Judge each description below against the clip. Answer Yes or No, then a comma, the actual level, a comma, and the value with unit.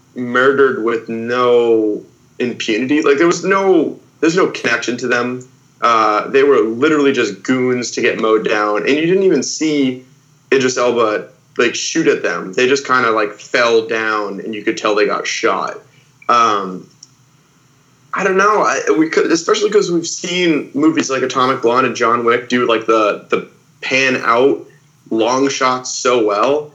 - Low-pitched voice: Yes, low, 130 Hz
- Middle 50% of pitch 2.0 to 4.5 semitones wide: No, average, 5.1 semitones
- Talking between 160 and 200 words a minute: Yes, average, 170 wpm